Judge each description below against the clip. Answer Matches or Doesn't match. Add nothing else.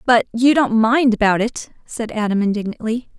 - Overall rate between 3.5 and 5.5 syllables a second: Matches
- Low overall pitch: Doesn't match